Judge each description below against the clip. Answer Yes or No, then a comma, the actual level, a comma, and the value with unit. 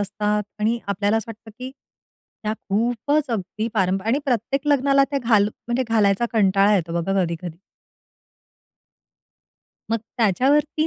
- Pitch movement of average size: Yes, average, 4.2 semitones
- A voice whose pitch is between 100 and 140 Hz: No, high, 220 Hz